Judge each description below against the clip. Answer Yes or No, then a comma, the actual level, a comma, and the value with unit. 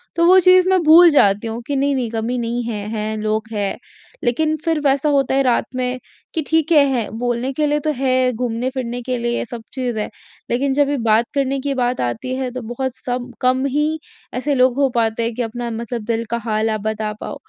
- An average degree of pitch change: Yes, average, 3.1 semitones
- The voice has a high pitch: Yes, very high, 250 Hz